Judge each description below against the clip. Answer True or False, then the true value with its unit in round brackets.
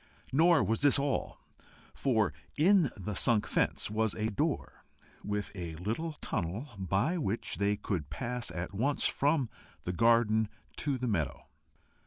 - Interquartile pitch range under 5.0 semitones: False (5.6 semitones)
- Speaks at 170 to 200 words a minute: False (145 wpm)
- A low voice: True (110 Hz)